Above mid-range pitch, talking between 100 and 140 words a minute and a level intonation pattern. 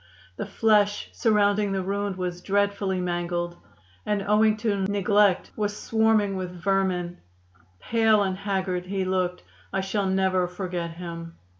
Yes: high, 195 Hz; slow, 135 wpm; narrow, 2.3 semitones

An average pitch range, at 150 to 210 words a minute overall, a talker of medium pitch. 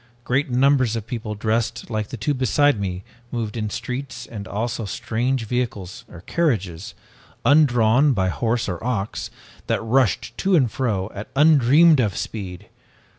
No: average, 3.9 semitones; average, 155 wpm; low, 115 Hz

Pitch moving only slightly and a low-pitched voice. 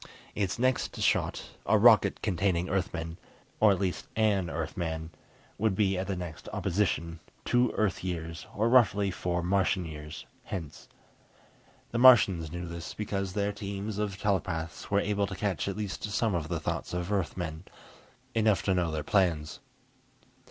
No: average, 3.3 semitones; very low, 95 Hz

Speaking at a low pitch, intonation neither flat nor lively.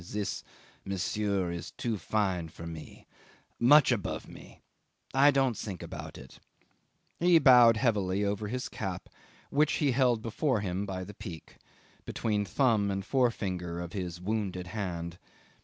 Yes: low, 105 Hz; average, 4.8 semitones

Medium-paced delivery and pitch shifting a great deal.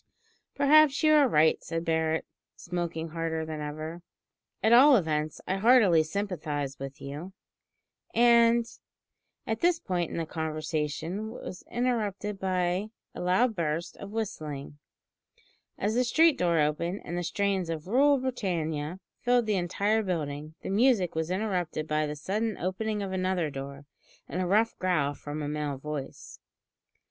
Yes: average, 150 wpm; wide, 5.7 semitones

